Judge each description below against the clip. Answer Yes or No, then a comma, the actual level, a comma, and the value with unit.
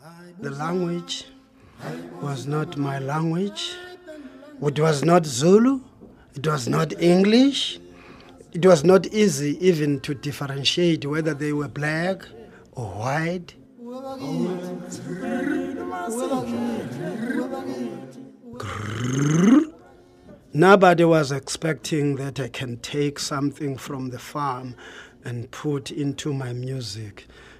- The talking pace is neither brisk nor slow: No, slow, 95 wpm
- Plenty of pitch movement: Yes, wide, 6.1 semitones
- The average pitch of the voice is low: No, medium, 155 Hz